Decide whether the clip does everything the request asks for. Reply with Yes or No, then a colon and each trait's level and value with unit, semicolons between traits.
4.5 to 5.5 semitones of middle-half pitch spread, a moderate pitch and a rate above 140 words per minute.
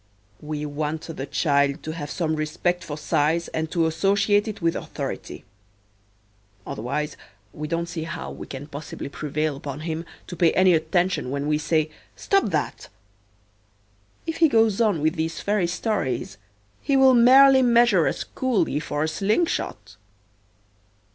Yes: average, 5.0 semitones; medium, 160 Hz; average, 150 wpm